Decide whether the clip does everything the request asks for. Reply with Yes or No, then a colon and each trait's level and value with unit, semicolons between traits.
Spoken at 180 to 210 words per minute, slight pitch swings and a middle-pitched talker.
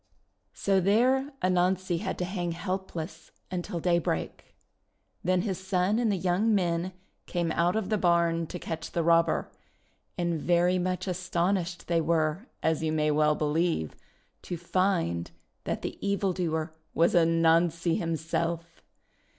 No: average, 140 wpm; narrow, 1.9 semitones; medium, 175 Hz